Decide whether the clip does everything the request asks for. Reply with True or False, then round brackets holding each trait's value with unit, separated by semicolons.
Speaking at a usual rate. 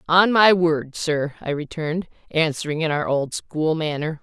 True (170 wpm)